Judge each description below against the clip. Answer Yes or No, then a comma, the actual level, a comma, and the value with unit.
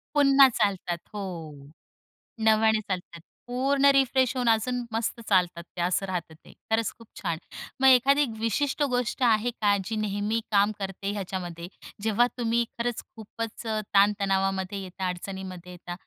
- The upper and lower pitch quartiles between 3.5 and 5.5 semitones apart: Yes, average, 3.9 semitones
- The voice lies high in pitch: Yes, high, 215 Hz